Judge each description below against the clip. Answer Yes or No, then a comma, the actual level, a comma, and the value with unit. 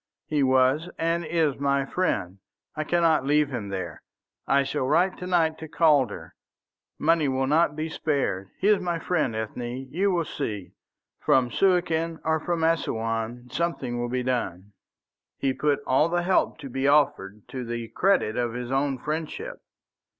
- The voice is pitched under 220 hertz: Yes, medium, 140 Hz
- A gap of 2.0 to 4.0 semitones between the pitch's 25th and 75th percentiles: No, average, 5.1 semitones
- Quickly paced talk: No, average, 165 wpm